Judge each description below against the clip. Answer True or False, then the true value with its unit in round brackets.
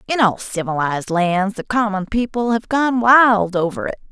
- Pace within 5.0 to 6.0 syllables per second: False (4.7 syllables/s)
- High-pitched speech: True (210 Hz)